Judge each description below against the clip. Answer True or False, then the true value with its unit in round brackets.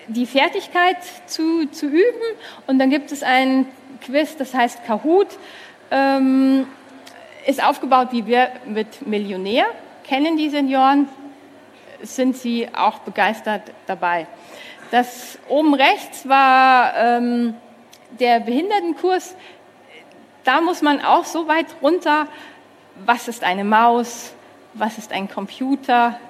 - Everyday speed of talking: False (115 wpm)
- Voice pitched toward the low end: False (265 Hz)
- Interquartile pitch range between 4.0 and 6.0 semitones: True (4.4 semitones)